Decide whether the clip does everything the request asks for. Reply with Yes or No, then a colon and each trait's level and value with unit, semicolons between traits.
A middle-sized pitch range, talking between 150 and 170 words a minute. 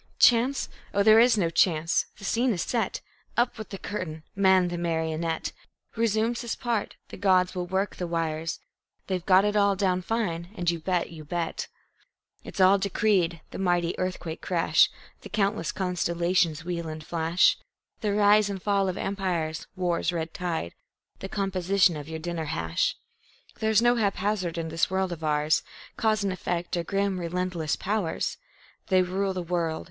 Yes: average, 3.1 semitones; average, 165 wpm